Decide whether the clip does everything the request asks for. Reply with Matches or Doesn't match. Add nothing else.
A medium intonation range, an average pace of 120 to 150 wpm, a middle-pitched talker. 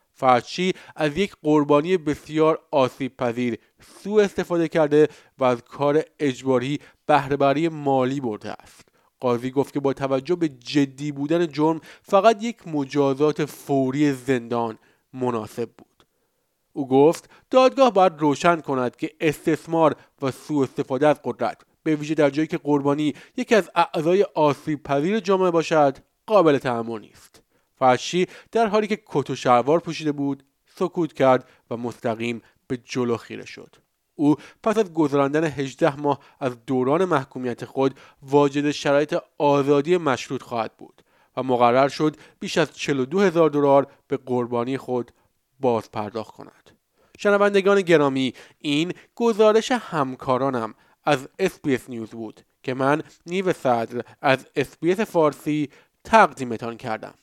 Matches